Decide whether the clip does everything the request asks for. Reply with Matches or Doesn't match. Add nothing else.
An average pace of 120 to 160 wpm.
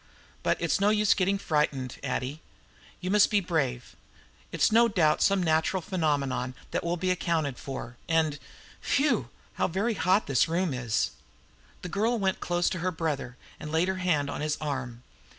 Doesn't match